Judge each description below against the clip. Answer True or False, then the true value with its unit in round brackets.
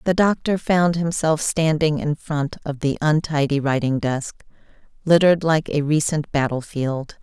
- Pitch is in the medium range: True (155 Hz)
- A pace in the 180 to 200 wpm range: False (140 wpm)